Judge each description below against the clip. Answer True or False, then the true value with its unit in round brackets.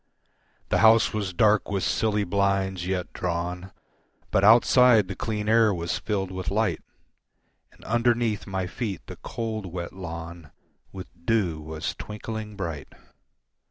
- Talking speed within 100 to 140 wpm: True (135 wpm)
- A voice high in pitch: False (95 Hz)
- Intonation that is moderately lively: True (3.6 semitones)